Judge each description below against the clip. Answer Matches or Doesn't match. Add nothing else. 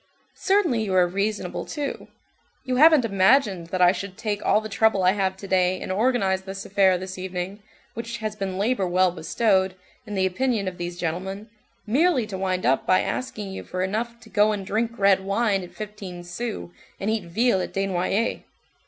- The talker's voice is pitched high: Matches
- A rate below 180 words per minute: Doesn't match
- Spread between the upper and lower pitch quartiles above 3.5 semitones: Doesn't match